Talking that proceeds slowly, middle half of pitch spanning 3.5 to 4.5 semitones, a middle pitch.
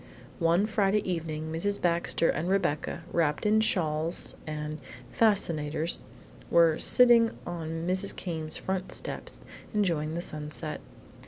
Yes: slow, 115 wpm; average, 3.8 semitones; medium, 170 Hz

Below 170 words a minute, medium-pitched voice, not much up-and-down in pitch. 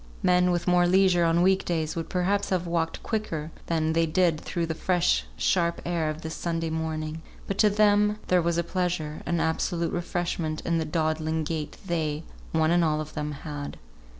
No: average, 190 wpm; medium, 165 Hz; narrow, 2.1 semitones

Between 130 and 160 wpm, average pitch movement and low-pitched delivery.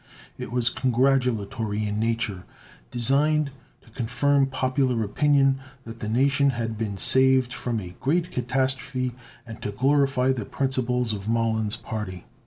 Yes: slow, 135 wpm; average, 3.1 semitones; low, 125 Hz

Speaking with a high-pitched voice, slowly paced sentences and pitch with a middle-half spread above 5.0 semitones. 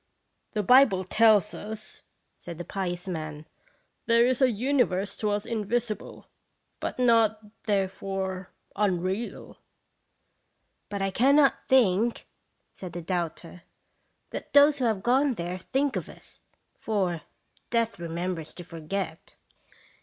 No: high, 205 Hz; slow, 130 wpm; average, 4.6 semitones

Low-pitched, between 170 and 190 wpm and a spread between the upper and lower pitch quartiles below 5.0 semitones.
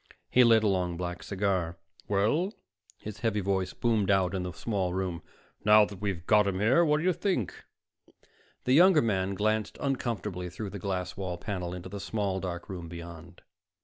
Yes: low, 100 Hz; average, 180 wpm; average, 3.3 semitones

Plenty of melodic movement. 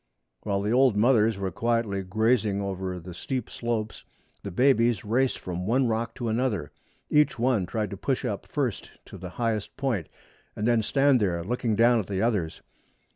No: average, 3.5 semitones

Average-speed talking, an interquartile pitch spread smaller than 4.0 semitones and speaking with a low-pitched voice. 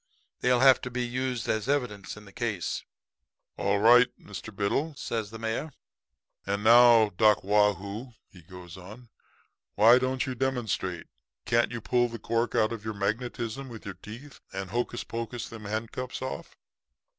Yes: average, 165 wpm; average, 3.0 semitones; low, 115 Hz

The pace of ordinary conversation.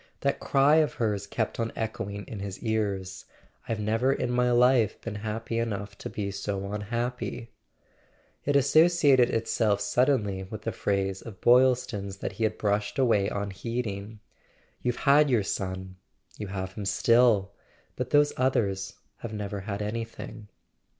Yes: average, 150 wpm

